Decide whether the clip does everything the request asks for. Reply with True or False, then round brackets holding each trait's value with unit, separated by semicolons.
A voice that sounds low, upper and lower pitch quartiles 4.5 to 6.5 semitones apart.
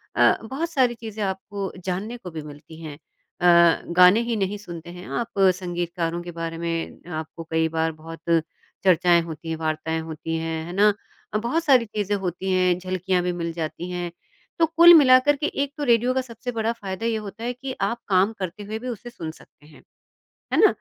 False (185 Hz; 5.6 semitones)